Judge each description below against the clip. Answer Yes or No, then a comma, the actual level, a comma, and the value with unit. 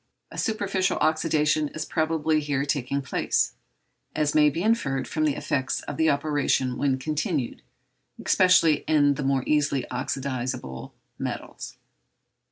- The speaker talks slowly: Yes, slow, 130 wpm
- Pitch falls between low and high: Yes, medium, 150 Hz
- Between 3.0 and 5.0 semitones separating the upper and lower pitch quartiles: No, narrow, 2.5 semitones